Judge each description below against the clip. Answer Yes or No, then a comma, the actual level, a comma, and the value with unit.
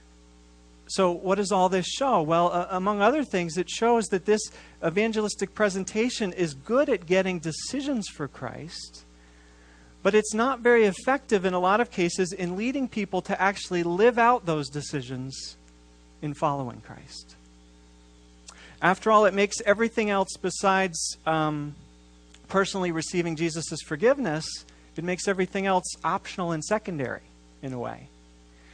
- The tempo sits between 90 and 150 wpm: Yes, average, 140 wpm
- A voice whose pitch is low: No, medium, 180 Hz